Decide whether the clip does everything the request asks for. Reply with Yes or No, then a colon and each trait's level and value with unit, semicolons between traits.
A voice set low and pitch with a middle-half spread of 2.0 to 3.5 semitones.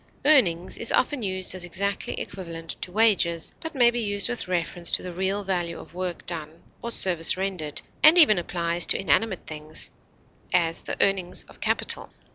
No: medium, 185 Hz; average, 3.1 semitones